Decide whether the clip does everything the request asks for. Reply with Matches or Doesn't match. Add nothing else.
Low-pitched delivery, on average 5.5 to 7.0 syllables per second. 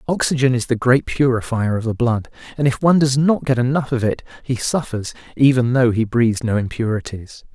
Matches